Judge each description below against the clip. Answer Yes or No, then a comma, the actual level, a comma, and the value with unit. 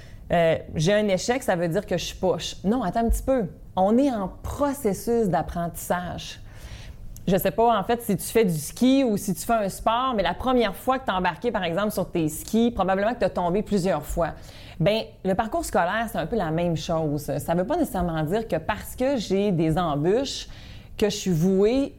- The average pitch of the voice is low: No, high, 200 Hz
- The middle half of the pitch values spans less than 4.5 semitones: No, average, 4.9 semitones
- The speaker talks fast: Yes, fast, 225 wpm